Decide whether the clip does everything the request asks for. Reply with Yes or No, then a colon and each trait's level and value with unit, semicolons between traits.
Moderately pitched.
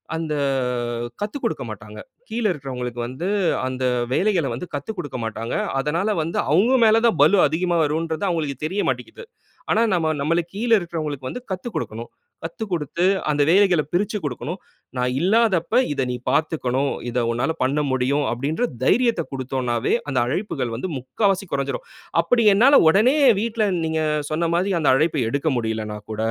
Yes: medium, 160 Hz